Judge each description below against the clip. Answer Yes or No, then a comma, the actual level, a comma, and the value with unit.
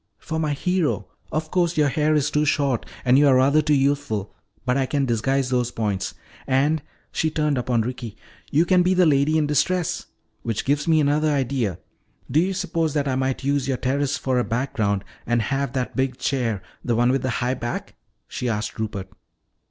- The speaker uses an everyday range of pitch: Yes, average, 3.5 semitones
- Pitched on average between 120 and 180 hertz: Yes, low, 135 Hz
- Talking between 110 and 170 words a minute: No, average, 200 wpm